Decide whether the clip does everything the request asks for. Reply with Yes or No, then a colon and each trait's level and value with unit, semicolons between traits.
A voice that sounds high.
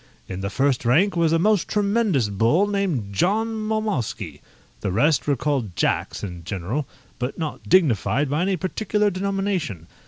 No: medium, 155 Hz